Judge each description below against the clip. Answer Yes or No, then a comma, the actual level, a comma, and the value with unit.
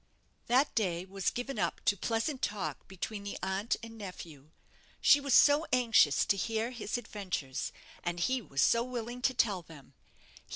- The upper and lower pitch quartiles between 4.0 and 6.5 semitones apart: Yes, average, 5.2 semitones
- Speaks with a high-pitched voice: Yes, high, 215 Hz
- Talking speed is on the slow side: No, average, 165 wpm